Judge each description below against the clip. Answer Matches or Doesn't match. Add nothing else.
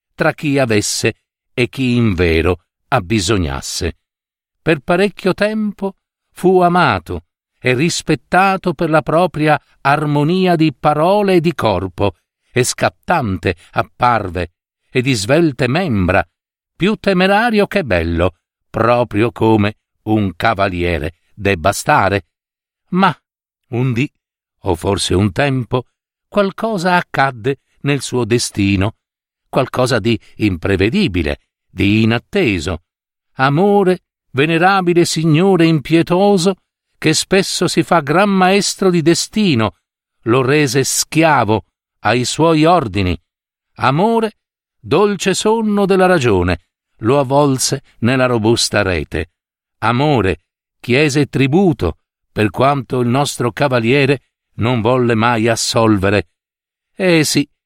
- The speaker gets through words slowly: Matches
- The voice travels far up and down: Matches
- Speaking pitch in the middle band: Doesn't match